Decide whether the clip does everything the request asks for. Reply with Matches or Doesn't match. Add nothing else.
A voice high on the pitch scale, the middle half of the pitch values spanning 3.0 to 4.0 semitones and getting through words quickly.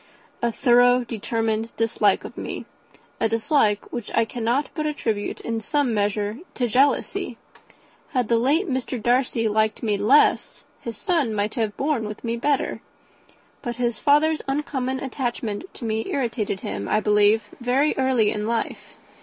Doesn't match